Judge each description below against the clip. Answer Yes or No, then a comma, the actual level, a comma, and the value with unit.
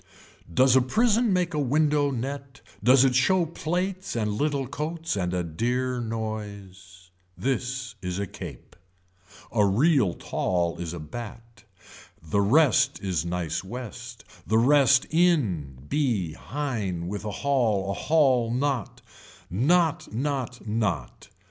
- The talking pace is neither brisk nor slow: No, slow, 130 wpm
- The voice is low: Yes, low, 120 Hz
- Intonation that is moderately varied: No, wide, 6.4 semitones